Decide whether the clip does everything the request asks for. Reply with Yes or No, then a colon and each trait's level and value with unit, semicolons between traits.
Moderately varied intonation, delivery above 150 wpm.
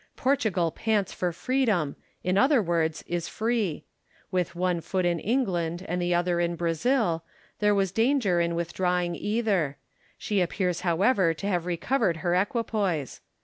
No: average, 3.6 semitones; average, 145 wpm